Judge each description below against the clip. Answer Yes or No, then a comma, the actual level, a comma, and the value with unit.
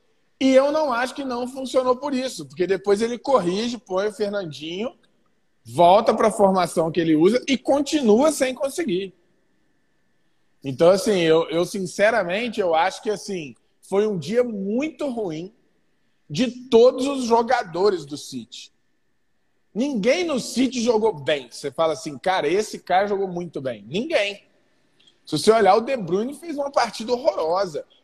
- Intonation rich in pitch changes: Yes, wide, 6.4 semitones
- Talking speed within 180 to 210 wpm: No, average, 155 wpm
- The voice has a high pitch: Yes, high, 210 Hz